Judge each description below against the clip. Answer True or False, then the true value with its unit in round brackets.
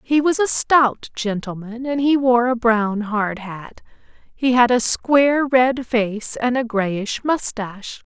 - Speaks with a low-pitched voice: False (240 Hz)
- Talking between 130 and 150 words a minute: False (165 wpm)